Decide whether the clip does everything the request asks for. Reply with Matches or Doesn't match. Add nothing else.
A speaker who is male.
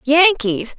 Doesn't match